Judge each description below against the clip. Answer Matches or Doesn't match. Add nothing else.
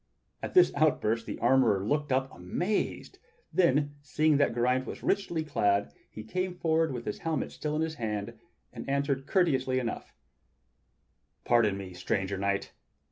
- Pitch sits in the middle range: Doesn't match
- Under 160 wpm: Matches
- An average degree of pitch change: Doesn't match